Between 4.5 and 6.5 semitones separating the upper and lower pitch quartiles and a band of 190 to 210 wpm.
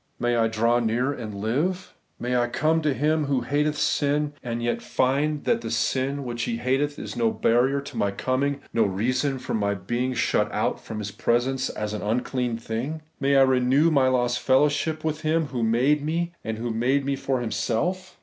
No: average, 3.6 semitones; average, 195 wpm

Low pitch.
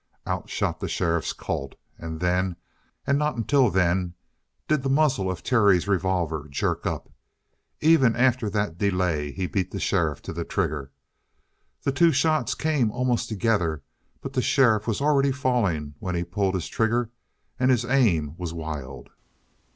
Yes: low, 100 Hz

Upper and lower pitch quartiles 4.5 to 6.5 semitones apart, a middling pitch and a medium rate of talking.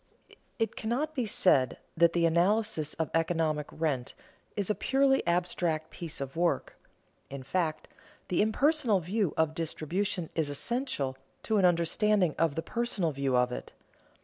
Yes: average, 5.3 semitones; medium, 170 Hz; average, 150 wpm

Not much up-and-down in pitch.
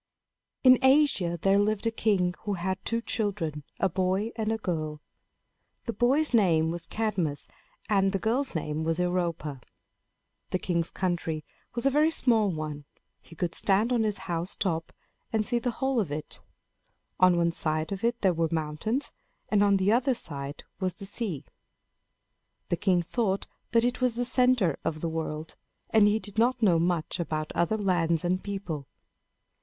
No: average, 5.2 semitones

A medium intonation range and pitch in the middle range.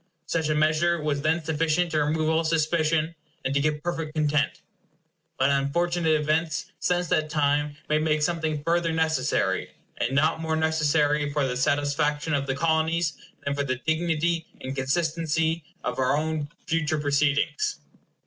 No: narrow, 1.9 semitones; medium, 155 Hz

